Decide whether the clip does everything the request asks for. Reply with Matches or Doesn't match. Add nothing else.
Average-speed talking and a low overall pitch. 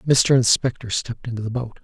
Matches